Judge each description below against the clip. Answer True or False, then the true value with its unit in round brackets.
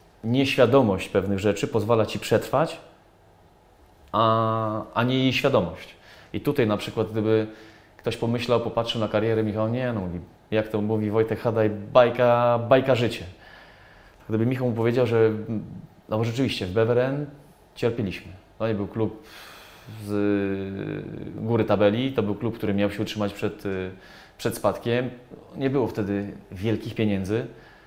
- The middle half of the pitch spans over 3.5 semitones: False (2.4 semitones)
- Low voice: True (110 Hz)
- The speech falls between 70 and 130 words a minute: False (140 wpm)